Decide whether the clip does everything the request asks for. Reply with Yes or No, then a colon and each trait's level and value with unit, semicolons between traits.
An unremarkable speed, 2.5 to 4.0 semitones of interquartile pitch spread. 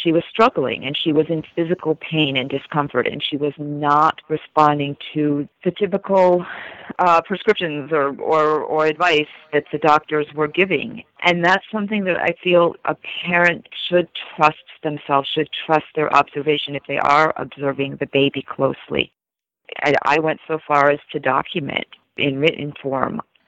Yes: average, 160 wpm; average, 3.0 semitones